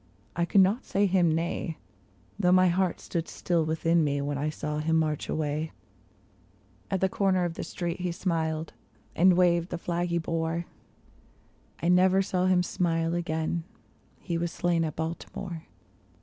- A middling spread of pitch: No, narrow, 2.0 semitones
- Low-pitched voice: No, medium, 170 Hz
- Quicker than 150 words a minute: Yes, average, 165 wpm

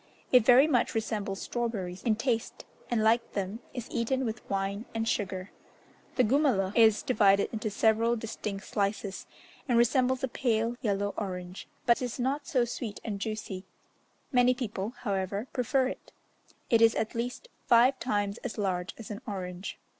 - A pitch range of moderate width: Yes, average, 3.5 semitones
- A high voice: Yes, high, 225 Hz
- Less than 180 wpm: Yes, average, 160 wpm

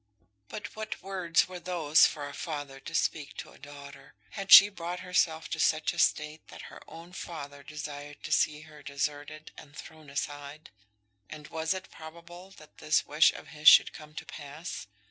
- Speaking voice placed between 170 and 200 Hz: No, medium, 155 Hz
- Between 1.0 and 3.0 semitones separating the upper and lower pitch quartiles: Yes, narrow, 2.6 semitones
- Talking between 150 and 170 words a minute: No, average, 185 wpm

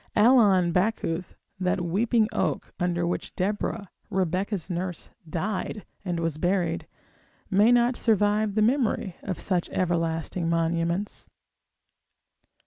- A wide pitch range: No, average, 3.5 semitones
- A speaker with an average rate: No, slow, 110 wpm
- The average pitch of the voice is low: No, medium, 185 Hz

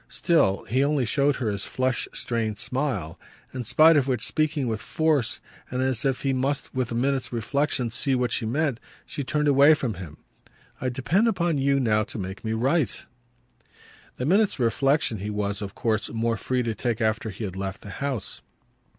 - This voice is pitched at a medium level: No, low, 125 Hz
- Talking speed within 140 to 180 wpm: No, average, 190 wpm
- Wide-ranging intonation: No, average, 4.2 semitones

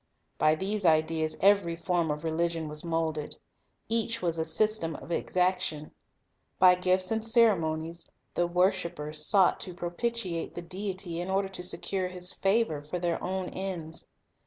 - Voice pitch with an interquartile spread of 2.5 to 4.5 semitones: Yes, average, 2.8 semitones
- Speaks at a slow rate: No, average, 155 wpm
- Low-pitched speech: No, medium, 175 Hz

